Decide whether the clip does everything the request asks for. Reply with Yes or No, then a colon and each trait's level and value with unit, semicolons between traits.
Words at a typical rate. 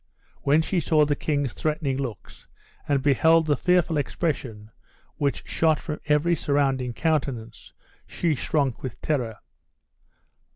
No: slow, 125 wpm